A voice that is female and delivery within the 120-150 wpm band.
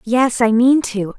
No: female; average, 200 wpm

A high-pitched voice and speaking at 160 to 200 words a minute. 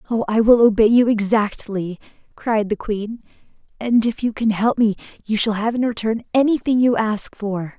Yes: high, 220 Hz; average, 185 wpm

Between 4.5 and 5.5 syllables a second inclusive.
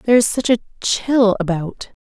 Yes: 4.7 syllables/s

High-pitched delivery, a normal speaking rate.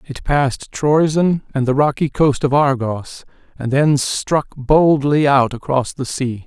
No: medium, 140 Hz; average, 160 wpm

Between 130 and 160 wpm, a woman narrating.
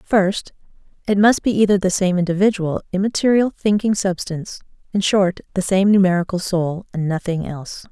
Yes: average, 150 wpm; female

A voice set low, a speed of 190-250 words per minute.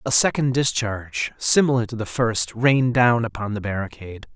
No: low, 115 Hz; average, 165 wpm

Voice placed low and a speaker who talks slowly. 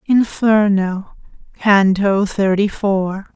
No: high, 200 Hz; slow, 70 wpm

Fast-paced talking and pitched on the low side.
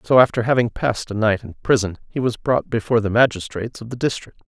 Yes: fast, 230 wpm; low, 115 Hz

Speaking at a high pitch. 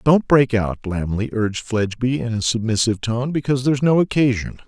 No: low, 120 Hz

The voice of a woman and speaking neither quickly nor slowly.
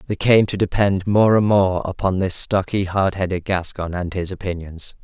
No: male; average, 190 wpm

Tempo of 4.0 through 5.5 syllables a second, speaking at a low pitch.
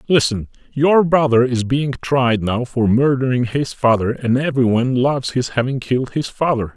Yes: 5.1 syllables/s; low, 130 Hz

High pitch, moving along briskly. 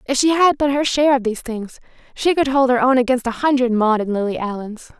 Yes: very high, 250 Hz; fast, 250 wpm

